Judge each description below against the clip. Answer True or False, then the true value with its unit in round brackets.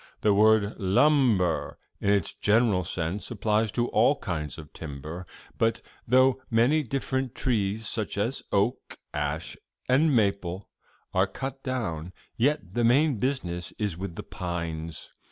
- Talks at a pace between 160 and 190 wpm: False (135 wpm)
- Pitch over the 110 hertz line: False (105 Hz)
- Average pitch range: False (6.1 semitones)